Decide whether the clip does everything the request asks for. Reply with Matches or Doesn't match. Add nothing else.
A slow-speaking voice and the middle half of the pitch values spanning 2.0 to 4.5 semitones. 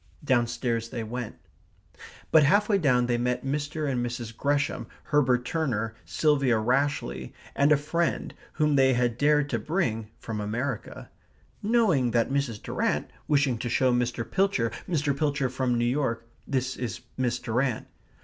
Doesn't match